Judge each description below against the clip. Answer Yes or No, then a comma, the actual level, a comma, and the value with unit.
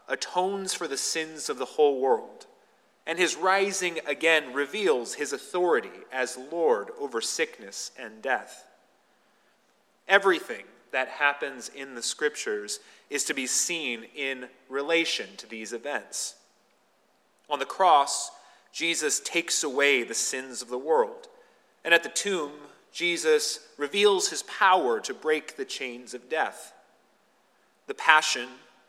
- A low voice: No, medium, 165 Hz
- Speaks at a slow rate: Yes, slow, 130 wpm